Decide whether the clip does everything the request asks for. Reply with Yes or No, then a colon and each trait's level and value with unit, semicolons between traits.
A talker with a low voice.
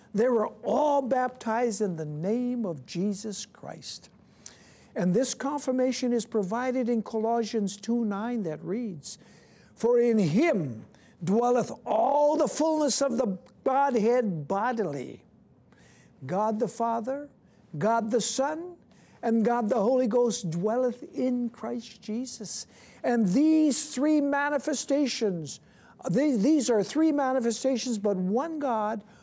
No: high, 235 Hz